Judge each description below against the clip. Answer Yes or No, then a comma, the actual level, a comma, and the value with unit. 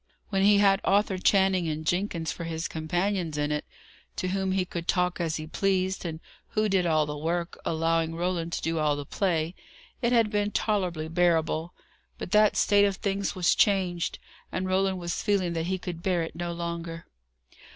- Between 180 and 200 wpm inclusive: Yes, average, 190 wpm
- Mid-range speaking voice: Yes, medium, 175 Hz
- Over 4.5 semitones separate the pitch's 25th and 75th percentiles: No, average, 2.9 semitones